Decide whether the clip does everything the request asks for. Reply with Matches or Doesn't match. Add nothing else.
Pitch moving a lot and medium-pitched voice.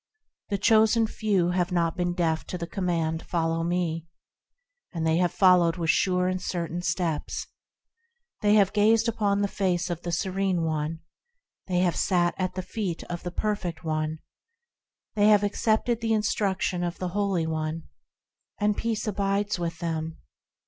Doesn't match